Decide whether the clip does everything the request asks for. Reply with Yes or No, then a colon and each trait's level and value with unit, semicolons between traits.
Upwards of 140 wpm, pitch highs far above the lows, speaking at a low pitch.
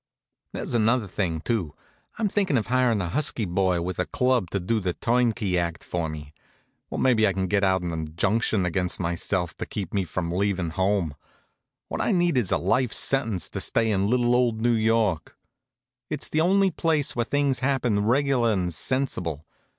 Yes: average, 185 wpm; wide, 5.8 semitones; low, 105 Hz